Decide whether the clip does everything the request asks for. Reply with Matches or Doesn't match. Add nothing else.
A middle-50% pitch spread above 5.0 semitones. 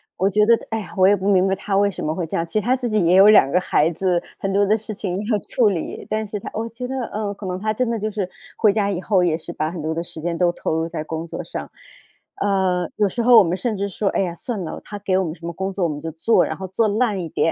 Doesn't match